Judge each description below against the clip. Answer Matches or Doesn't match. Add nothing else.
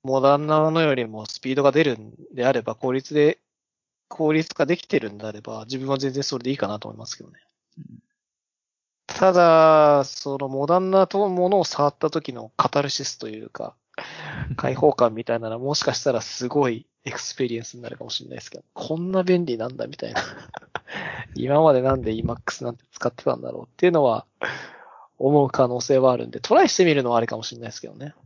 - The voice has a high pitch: Doesn't match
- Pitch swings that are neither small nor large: Matches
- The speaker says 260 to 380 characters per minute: Doesn't match